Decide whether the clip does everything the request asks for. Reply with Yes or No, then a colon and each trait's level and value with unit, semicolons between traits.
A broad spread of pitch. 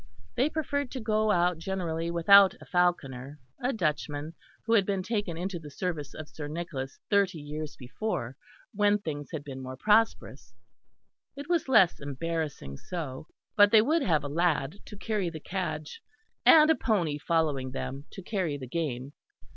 Yes: wide, 5.8 semitones